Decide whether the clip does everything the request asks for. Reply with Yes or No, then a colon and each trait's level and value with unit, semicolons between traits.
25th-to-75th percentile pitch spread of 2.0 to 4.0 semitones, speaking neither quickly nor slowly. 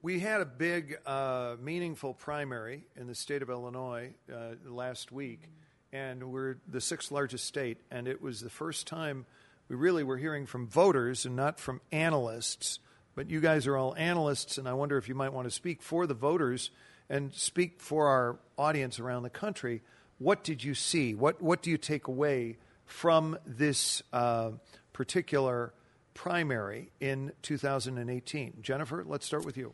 Yes: average, 3.7 semitones; average, 180 wpm